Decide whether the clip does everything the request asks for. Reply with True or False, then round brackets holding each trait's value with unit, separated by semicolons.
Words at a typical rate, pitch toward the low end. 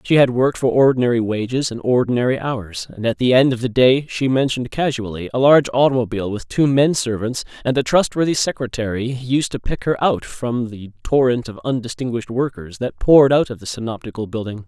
True (190 wpm; 125 Hz)